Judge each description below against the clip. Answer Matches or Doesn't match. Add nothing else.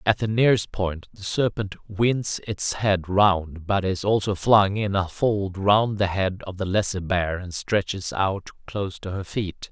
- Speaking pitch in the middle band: Doesn't match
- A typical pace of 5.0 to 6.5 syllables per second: Doesn't match